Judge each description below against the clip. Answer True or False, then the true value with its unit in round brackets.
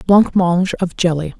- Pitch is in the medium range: True (175 Hz)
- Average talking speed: False (130 wpm)